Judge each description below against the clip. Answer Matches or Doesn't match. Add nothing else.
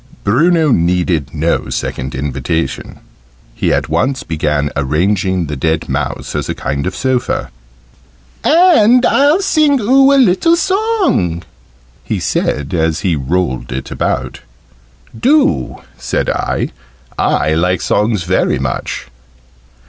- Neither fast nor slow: Doesn't match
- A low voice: Matches